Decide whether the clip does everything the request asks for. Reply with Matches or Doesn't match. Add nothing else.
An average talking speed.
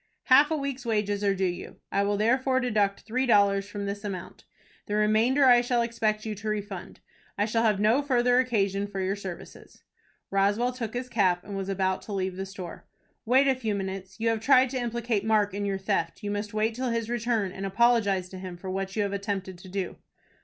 Doesn't match